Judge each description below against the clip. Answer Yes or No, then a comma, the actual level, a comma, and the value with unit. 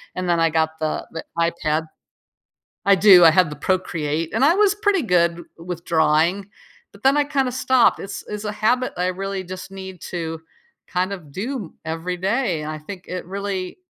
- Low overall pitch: No, medium, 185 Hz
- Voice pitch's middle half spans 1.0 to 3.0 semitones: No, average, 3.8 semitones